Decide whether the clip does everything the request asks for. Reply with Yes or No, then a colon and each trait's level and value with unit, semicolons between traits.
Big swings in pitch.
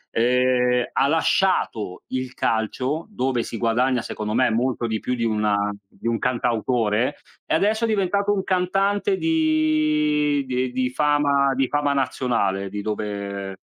Yes: wide, 5.8 semitones